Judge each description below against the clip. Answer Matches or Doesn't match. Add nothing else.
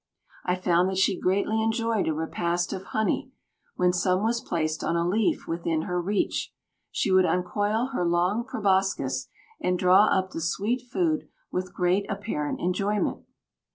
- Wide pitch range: Doesn't match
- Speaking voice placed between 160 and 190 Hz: Matches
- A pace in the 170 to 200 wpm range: Doesn't match